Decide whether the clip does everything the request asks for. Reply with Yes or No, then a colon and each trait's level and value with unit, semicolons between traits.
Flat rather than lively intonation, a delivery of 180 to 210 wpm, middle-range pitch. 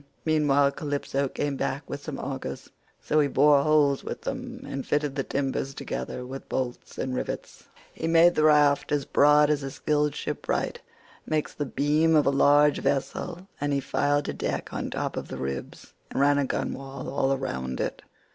Yes: narrow, 1.6 semitones; average, 185 wpm; medium, 145 Hz